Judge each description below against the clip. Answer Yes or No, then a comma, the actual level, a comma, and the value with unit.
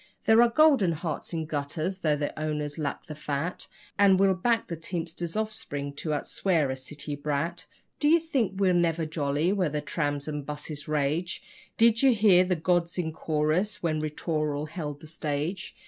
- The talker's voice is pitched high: No, medium, 160 Hz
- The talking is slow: No, average, 180 wpm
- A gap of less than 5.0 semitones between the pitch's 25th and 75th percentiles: Yes, average, 4.0 semitones